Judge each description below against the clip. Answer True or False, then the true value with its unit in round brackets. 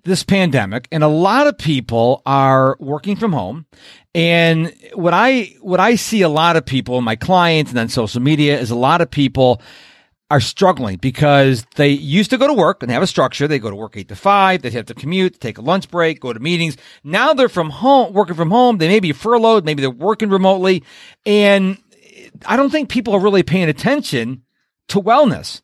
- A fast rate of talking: True (210 wpm)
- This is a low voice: False (170 Hz)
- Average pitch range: False (7.0 semitones)